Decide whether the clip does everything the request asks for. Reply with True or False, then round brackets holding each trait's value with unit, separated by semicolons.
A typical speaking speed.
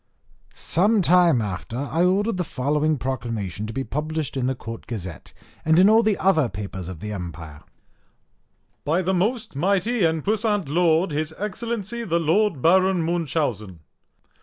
True (160 wpm)